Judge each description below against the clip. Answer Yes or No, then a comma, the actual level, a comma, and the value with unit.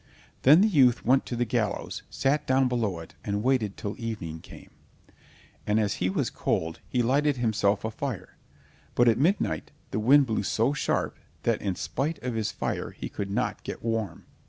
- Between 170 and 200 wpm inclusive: Yes, average, 185 wpm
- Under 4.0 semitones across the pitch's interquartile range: No, average, 4.4 semitones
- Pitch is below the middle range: Yes, low, 115 Hz